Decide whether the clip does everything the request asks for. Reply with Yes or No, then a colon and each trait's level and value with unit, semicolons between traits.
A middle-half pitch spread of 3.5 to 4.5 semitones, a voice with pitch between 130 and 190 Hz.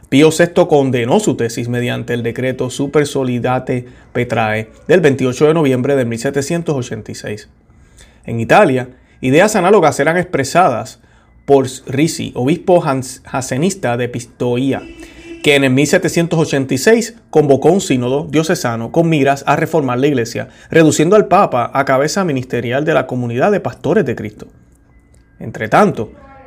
Yes: average, 4.2 semitones; low, 135 Hz